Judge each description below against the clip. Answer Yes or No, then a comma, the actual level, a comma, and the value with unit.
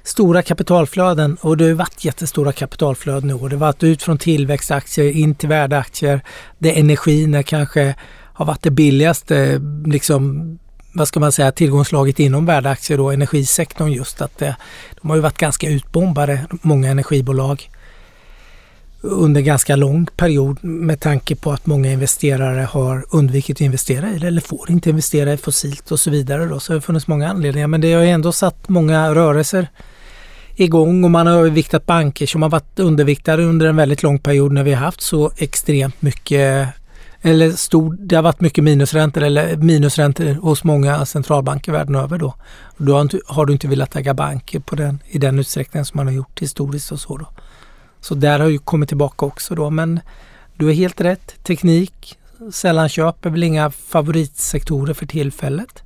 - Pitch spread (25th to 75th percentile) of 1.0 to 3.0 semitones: Yes, narrow, 2.4 semitones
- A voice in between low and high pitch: Yes, medium, 150 Hz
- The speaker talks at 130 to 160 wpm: No, average, 180 wpm